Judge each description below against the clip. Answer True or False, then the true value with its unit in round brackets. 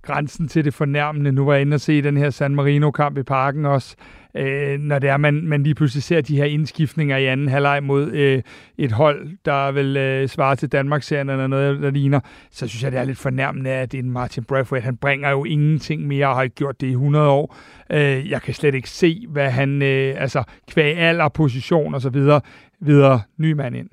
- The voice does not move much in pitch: True (1.6 semitones)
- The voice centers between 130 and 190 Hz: True (140 Hz)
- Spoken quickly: True (230 wpm)